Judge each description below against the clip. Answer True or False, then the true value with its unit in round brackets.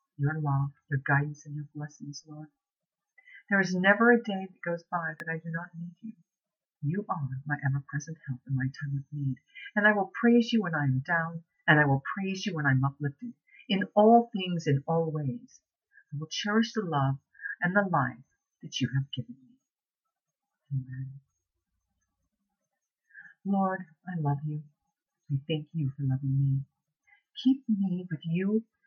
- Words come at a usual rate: True (175 wpm)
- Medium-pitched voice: True (160 Hz)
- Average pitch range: False (6.2 semitones)